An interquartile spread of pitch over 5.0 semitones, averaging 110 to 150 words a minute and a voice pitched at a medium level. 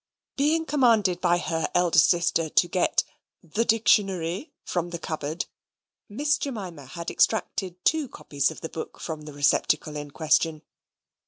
Yes: wide, 5.4 semitones; average, 145 wpm; medium, 175 Hz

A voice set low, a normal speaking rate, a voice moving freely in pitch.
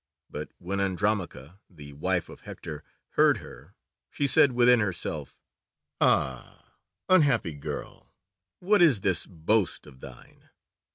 No: very low, 95 Hz; slow, 120 wpm; wide, 7.1 semitones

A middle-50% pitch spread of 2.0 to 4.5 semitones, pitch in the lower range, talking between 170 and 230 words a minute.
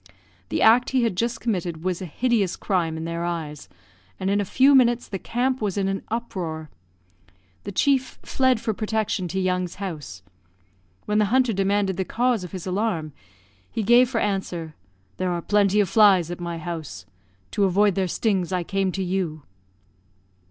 No: average, 4.2 semitones; high, 195 Hz; average, 180 wpm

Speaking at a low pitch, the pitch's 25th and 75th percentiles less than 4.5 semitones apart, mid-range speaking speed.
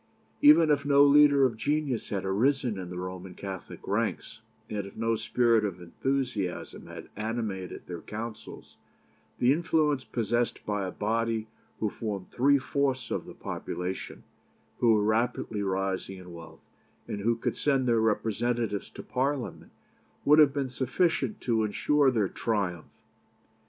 No: low, 115 Hz; average, 4.9 semitones; average, 145 wpm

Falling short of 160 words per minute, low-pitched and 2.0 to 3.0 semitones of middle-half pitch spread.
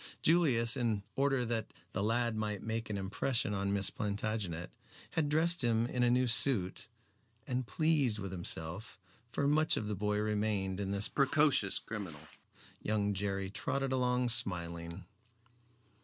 No: average, 145 wpm; low, 110 Hz; average, 4.0 semitones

